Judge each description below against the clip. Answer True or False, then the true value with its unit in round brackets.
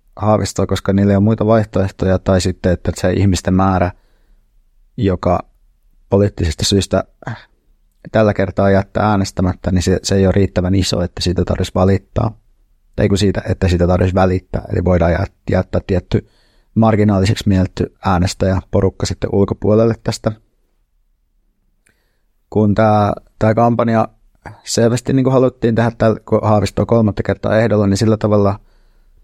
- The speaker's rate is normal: True (130 wpm)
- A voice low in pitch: True (100 Hz)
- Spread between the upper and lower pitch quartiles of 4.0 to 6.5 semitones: False (2.8 semitones)